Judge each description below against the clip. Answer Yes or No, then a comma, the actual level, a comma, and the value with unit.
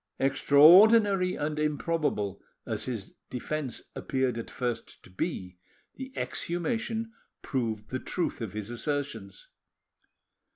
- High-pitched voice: No, low, 135 Hz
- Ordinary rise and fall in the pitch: No, wide, 7.1 semitones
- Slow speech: Yes, slow, 110 wpm